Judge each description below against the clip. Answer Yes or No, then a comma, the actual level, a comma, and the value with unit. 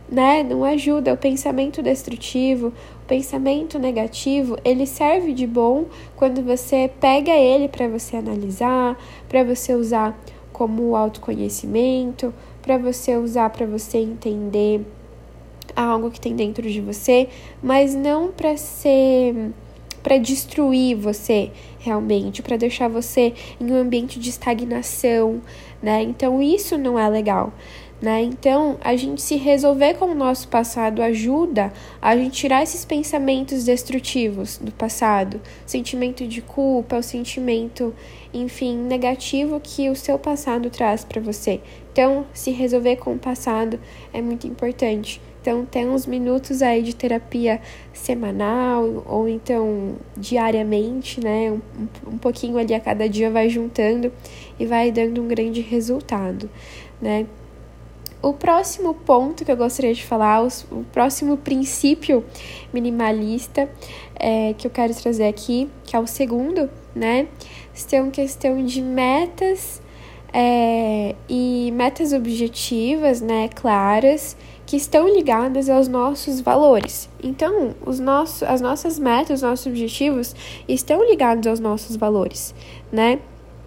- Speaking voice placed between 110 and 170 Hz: No, high, 245 Hz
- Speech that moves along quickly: No, average, 130 wpm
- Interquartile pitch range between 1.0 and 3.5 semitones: Yes, average, 3.0 semitones